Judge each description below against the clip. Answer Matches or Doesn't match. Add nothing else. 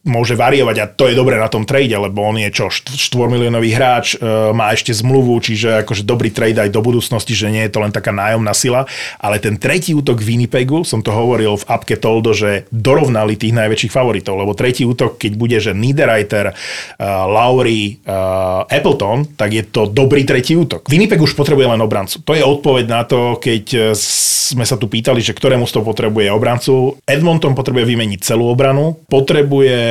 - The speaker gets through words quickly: Matches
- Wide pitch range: Doesn't match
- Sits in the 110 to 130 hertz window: Matches